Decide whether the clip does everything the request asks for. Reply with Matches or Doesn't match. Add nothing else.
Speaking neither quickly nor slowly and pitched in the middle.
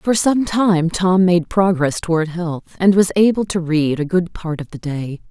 Doesn't match